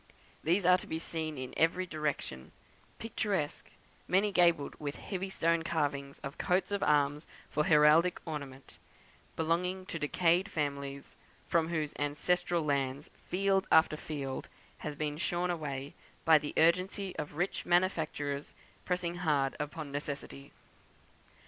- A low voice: No, medium, 160 Hz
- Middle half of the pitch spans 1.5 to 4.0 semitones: Yes, average, 3.5 semitones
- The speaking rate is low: Yes, slow, 130 wpm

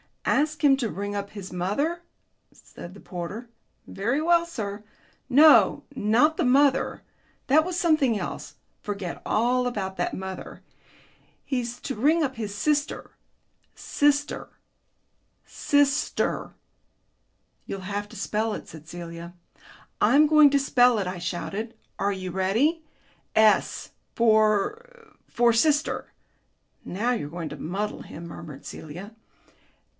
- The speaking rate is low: Yes, slow, 125 wpm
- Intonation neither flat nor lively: No, wide, 6.7 semitones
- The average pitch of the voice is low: No, high, 225 Hz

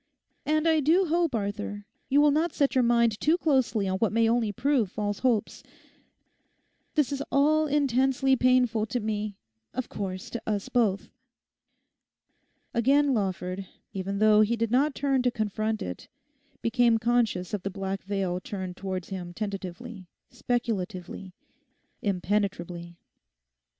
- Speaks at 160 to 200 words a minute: No, average, 140 wpm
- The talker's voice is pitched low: No, high, 220 Hz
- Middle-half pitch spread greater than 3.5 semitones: Yes, average, 4.8 semitones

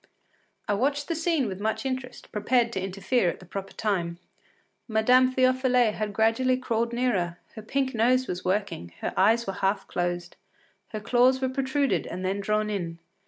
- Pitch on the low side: No, high, 220 Hz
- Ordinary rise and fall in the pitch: Yes, average, 4.8 semitones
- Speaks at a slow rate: No, average, 175 wpm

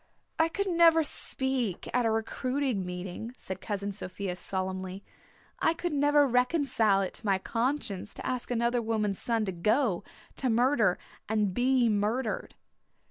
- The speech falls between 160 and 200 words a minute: No, average, 145 wpm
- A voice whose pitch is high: Yes, high, 230 Hz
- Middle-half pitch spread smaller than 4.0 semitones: No, average, 5.0 semitones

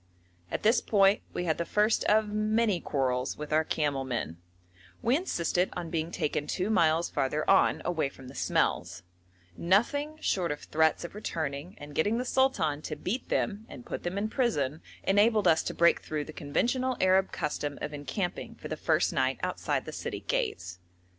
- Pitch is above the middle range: No, medium, 170 Hz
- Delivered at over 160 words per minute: Yes, average, 180 wpm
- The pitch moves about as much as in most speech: No, wide, 6.2 semitones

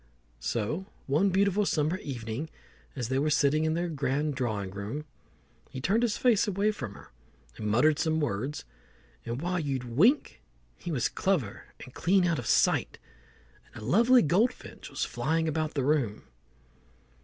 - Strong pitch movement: Yes, wide, 6.2 semitones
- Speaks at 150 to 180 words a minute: Yes, average, 160 wpm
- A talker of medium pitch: Yes, medium, 150 Hz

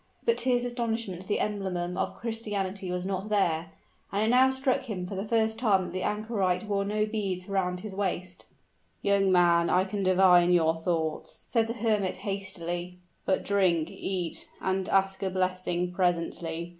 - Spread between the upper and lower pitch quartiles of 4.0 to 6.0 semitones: No, average, 2.8 semitones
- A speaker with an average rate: Yes, average, 170 wpm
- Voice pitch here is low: No, high, 190 Hz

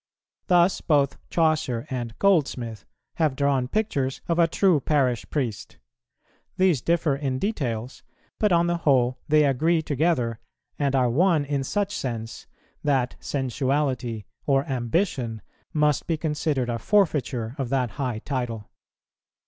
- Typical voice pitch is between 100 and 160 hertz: Yes, medium, 140 Hz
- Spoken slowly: Yes, slow, 130 wpm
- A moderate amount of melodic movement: Yes, average, 4.5 semitones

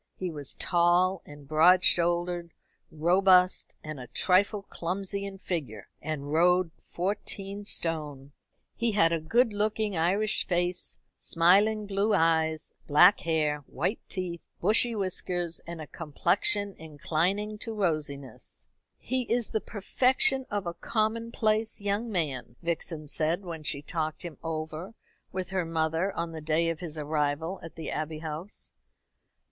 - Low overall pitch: No, medium, 175 Hz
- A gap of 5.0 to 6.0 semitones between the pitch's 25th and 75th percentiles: No, average, 4.0 semitones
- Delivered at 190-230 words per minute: No, average, 140 wpm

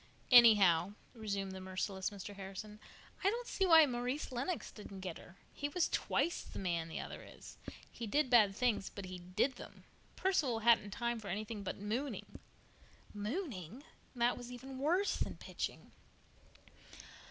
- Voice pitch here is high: Yes, high, 220 Hz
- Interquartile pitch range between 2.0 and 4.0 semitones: No, average, 5.2 semitones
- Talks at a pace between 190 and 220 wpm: No, average, 155 wpm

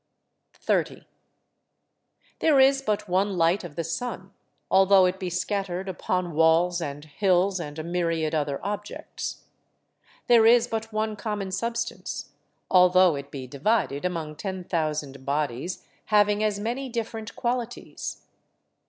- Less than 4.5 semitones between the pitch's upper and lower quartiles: No, average, 4.8 semitones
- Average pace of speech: No, slow, 130 wpm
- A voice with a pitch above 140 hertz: Yes, medium, 185 Hz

